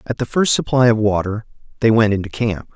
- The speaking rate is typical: No, fast, 220 wpm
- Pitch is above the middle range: No, low, 115 Hz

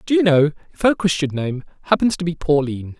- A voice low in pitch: No, medium, 160 Hz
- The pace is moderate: No, fast, 220 wpm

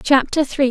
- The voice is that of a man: No, female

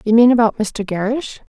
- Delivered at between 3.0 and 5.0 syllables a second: No, 5.2 syllables/s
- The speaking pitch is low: No, high, 225 Hz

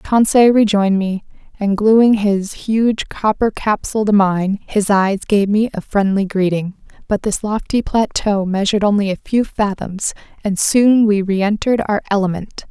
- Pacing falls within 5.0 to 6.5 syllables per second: No, 4.5 syllables/s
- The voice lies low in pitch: No, high, 205 Hz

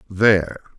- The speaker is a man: Yes, male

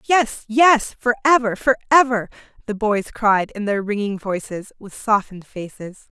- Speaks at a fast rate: No, average, 155 wpm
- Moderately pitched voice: No, high, 220 Hz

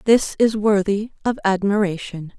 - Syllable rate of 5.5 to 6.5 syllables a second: No, 4.5 syllables/s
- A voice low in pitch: No, high, 200 Hz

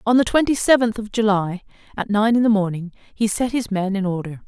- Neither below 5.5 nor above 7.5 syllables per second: Yes, 5.6 syllables/s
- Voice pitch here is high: Yes, high, 210 Hz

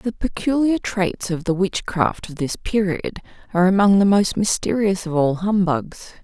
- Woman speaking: Yes, female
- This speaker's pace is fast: No, average, 165 wpm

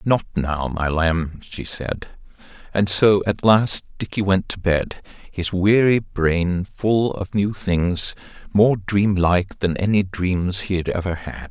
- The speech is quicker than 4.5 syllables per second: No, 3.5 syllables/s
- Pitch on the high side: No, very low, 95 Hz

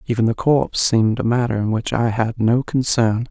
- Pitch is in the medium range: No, low, 115 Hz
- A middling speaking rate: No, fast, 220 wpm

